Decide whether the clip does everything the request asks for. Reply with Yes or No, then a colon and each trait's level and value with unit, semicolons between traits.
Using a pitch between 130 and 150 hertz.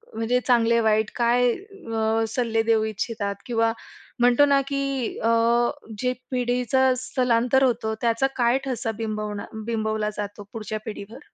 No: high, 230 Hz